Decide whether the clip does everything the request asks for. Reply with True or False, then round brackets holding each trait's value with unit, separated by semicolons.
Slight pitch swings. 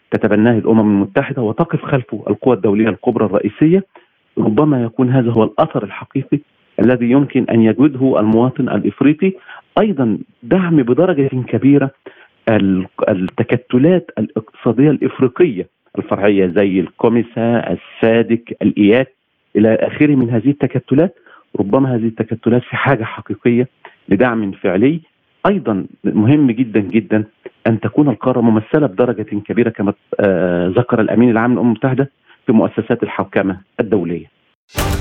False (3.8 semitones)